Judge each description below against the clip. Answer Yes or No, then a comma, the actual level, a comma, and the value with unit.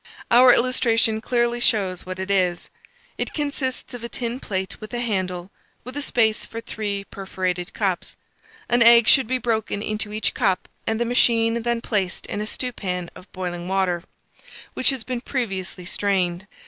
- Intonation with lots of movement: No, average, 4.1 semitones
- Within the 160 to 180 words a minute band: Yes, average, 170 wpm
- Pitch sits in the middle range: No, high, 220 Hz